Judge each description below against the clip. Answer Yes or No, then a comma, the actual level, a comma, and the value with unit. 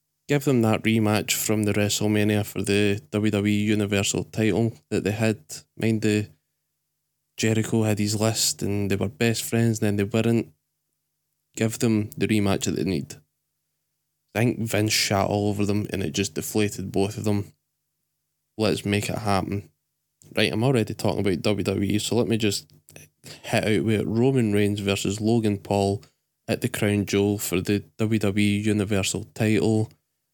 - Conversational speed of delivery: Yes, average, 165 wpm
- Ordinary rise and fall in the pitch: No, narrow, 2.3 semitones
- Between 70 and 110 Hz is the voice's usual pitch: Yes, low, 105 Hz